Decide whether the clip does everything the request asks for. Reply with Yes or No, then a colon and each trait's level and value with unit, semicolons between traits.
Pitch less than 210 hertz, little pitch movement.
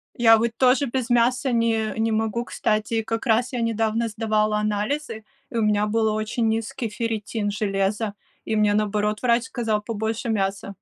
No: high, 220 Hz; narrow, 1.7 semitones